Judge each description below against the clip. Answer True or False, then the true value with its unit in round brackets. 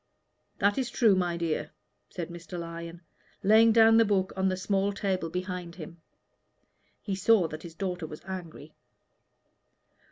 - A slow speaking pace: False (150 wpm)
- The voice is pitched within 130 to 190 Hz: True (185 Hz)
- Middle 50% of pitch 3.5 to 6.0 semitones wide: False (2.9 semitones)